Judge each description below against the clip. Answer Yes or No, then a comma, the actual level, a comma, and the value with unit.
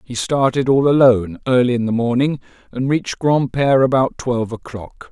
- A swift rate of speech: No, average, 165 wpm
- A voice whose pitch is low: Yes, low, 125 Hz